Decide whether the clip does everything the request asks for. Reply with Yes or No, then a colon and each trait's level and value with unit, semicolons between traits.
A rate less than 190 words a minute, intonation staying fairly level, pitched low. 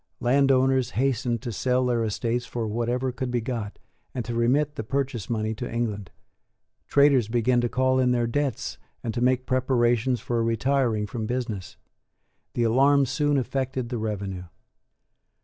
Yes: average, 155 wpm; narrow, 2.3 semitones; low, 120 Hz